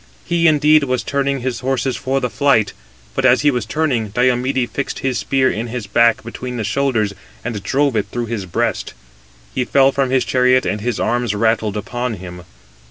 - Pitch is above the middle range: No, low, 125 Hz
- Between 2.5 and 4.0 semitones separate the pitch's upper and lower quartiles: Yes, average, 3.2 semitones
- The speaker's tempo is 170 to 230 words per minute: Yes, average, 185 wpm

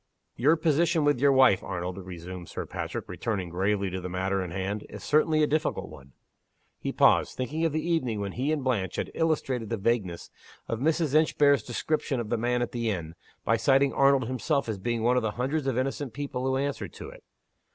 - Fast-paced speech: Yes, fast, 210 wpm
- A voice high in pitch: No, low, 125 Hz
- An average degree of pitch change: No, wide, 6.5 semitones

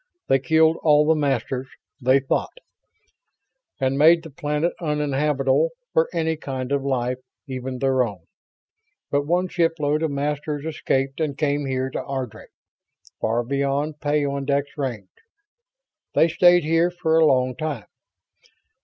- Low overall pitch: No, medium, 145 Hz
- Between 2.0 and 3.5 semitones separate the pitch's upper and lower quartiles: Yes, average, 2.9 semitones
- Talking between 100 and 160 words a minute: Yes, slow, 135 wpm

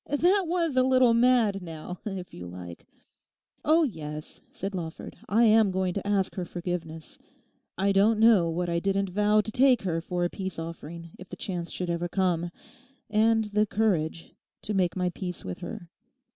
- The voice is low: No, high, 190 Hz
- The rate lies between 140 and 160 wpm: No, average, 170 wpm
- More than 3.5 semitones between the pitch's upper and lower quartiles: Yes, average, 4.4 semitones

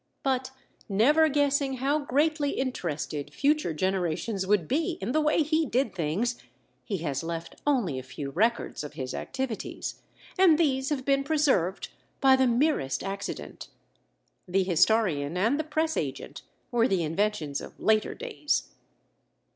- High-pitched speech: Yes, high, 235 Hz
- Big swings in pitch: Yes, wide, 8.4 semitones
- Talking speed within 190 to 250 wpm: No, average, 145 wpm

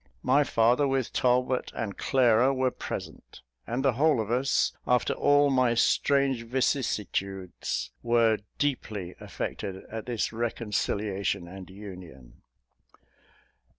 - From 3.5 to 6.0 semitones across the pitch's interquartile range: Yes, average, 4.5 semitones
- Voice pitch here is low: Yes, low, 120 Hz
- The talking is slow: Yes, slow, 115 wpm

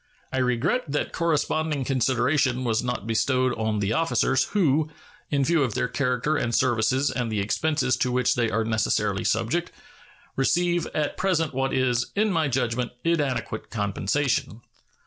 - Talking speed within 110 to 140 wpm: No, average, 150 wpm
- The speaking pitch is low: Yes, low, 130 Hz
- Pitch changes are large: No, average, 4.5 semitones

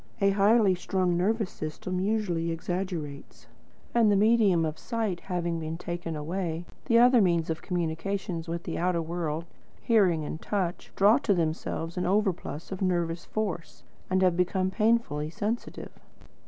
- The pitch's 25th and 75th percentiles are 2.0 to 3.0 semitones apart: No, average, 3.4 semitones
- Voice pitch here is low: No, medium, 180 Hz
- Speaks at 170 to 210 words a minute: No, average, 150 wpm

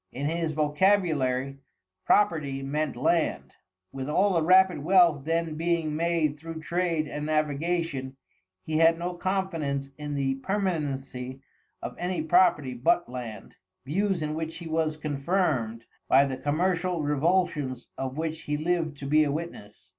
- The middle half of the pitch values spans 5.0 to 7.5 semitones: No, average, 3.7 semitones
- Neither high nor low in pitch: Yes, medium, 155 Hz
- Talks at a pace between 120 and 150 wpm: Yes, average, 145 wpm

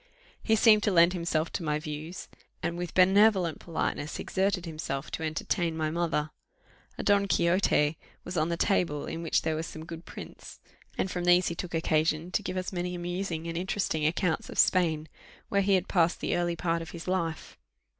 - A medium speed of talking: Yes, average, 195 wpm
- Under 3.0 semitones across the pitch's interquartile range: Yes, narrow, 2.4 semitones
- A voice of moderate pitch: Yes, medium, 170 Hz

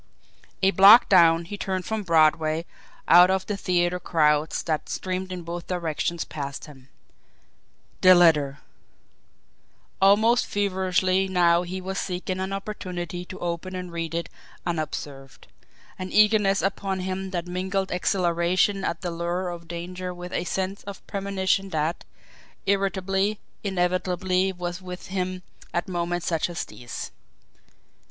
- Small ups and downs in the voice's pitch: Yes, narrow, 1.9 semitones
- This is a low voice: No, medium, 180 Hz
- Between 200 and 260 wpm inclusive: No, slow, 135 wpm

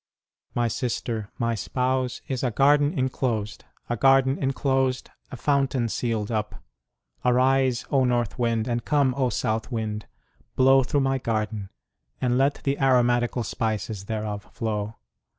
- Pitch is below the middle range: Yes, low, 125 Hz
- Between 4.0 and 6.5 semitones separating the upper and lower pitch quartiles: No, average, 3.1 semitones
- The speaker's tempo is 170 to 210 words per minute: No, slow, 135 wpm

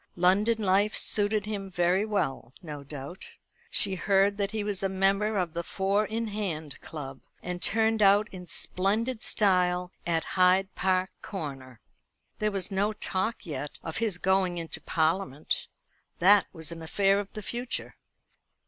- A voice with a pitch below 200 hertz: Yes, high, 190 Hz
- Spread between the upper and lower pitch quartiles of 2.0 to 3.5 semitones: Yes, average, 3.2 semitones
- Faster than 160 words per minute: No, average, 155 wpm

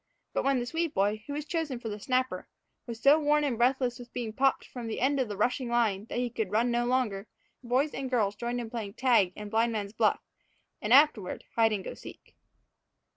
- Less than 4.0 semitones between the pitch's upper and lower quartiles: Yes, average, 3.2 semitones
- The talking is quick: Yes, fast, 225 wpm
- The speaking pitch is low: No, high, 240 Hz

